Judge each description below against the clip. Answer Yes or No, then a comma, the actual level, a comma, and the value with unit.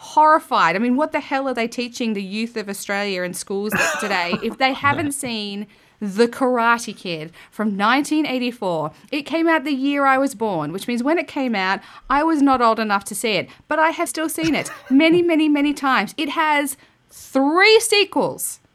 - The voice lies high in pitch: Yes, very high, 260 Hz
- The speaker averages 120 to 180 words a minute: No, average, 195 wpm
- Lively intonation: Yes, wide, 6.3 semitones